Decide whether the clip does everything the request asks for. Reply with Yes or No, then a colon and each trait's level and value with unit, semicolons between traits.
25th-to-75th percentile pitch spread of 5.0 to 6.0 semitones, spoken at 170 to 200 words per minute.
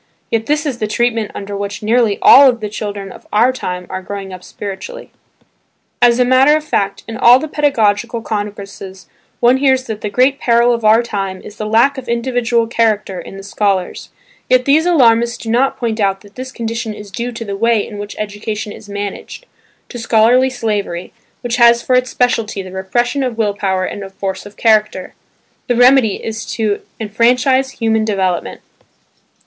No: average, 3.2 semitones; average, 185 wpm